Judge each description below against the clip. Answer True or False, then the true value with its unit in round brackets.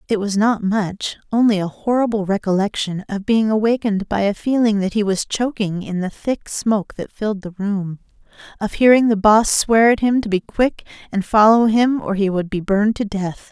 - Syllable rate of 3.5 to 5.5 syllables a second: True (5.1 syllables/s)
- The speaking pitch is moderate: False (210 Hz)